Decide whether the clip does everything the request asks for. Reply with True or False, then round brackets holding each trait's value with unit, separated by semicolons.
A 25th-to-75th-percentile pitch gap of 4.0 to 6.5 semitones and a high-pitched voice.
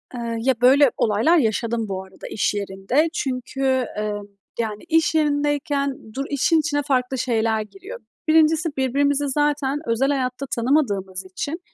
True (4.5 semitones; 265 Hz)